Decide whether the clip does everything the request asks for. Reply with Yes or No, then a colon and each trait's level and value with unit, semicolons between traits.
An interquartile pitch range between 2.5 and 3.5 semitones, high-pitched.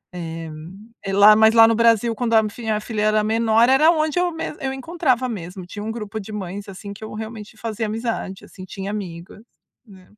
Yes: average, 2.8 semitones; high, 215 Hz